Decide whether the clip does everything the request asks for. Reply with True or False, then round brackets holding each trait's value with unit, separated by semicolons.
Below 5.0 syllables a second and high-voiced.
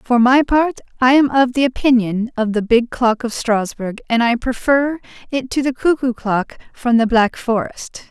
True (4.5 syllables/s; 245 Hz)